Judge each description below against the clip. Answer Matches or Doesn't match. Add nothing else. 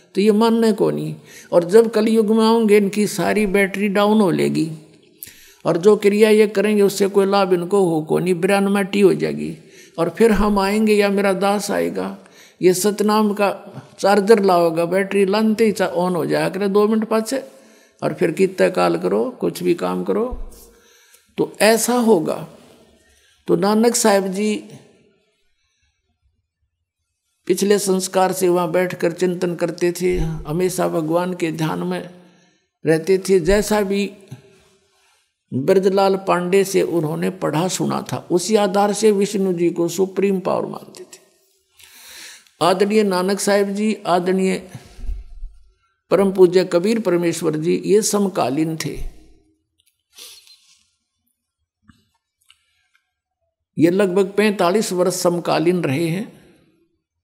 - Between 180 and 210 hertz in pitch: Matches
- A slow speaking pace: Doesn't match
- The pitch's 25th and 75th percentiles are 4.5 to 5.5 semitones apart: Doesn't match